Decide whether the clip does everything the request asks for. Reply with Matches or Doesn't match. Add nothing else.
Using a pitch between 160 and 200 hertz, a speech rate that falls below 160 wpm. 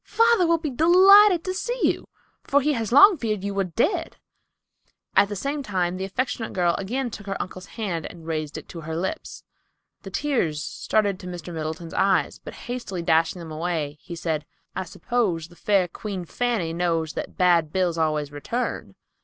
Doesn't match